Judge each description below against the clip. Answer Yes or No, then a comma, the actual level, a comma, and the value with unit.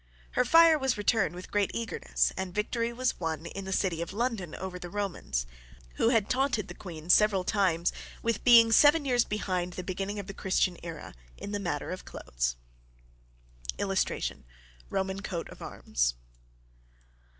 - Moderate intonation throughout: Yes, average, 4.4 semitones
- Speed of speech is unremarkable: Yes, average, 160 wpm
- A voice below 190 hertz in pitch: No, high, 195 Hz